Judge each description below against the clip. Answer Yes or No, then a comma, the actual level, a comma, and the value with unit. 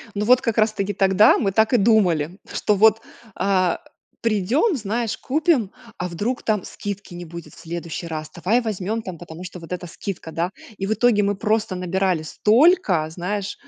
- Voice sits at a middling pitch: No, high, 200 Hz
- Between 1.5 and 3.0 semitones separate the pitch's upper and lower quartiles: No, average, 3.8 semitones